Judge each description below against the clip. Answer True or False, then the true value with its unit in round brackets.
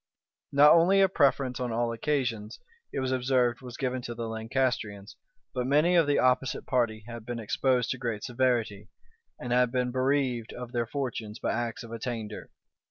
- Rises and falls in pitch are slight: True (2.3 semitones)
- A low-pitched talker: True (125 Hz)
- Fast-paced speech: False (175 wpm)